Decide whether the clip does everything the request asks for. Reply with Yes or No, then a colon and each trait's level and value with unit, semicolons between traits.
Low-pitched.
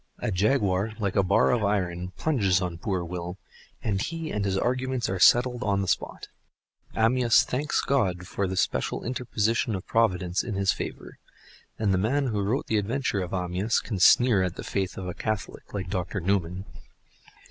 Yes: low, 100 Hz